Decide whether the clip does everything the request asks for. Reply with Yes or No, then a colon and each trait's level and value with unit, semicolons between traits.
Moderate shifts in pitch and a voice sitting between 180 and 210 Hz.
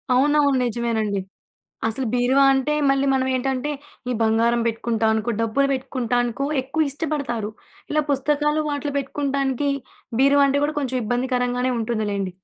No: average, 3.0 semitones; very high, 260 Hz